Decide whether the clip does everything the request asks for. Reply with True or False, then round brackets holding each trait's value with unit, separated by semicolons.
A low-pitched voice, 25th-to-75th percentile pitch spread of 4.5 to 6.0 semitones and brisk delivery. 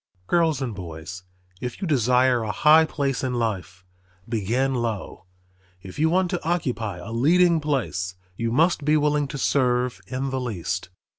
False (125 Hz; 5.4 semitones; 160 wpm)